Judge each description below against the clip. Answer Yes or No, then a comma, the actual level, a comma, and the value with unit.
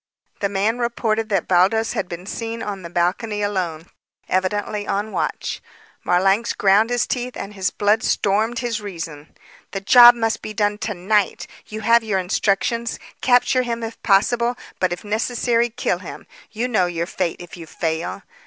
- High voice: Yes, high, 210 Hz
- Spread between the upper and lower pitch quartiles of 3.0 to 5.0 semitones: Yes, average, 3.7 semitones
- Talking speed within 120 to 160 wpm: No, average, 170 wpm